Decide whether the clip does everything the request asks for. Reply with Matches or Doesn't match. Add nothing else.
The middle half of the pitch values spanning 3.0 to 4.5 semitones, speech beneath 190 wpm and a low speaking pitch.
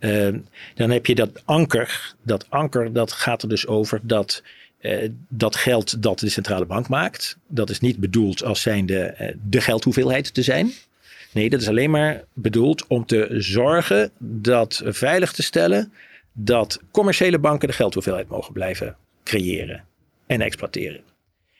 Matches